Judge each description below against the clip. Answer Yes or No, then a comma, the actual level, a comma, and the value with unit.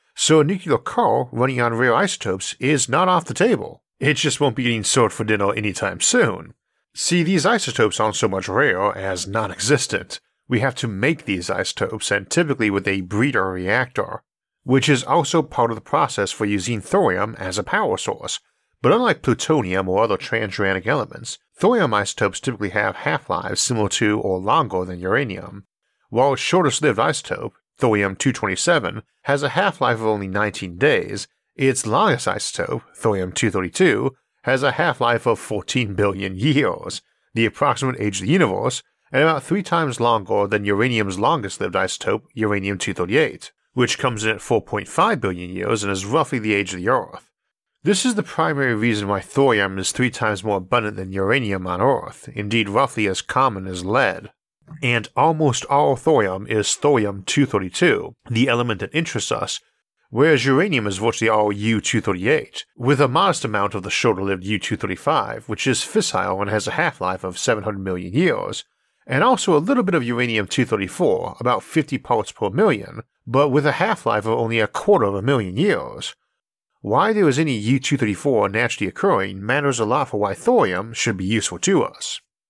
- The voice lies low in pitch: Yes, low, 110 Hz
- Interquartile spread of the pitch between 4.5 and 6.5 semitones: Yes, wide, 5.4 semitones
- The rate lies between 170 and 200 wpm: Yes, average, 180 wpm